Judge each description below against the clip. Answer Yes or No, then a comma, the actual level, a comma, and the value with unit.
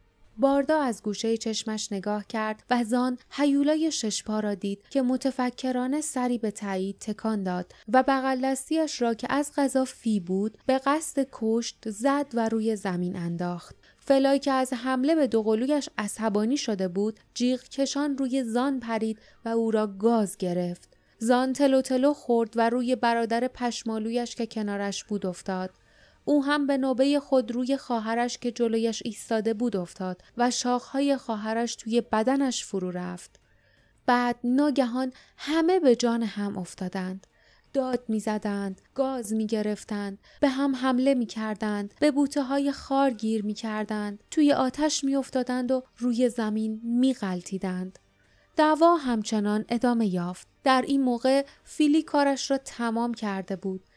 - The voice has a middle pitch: No, high, 240 Hz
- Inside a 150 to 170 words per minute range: No, average, 140 wpm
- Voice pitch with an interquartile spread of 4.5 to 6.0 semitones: No, average, 3.9 semitones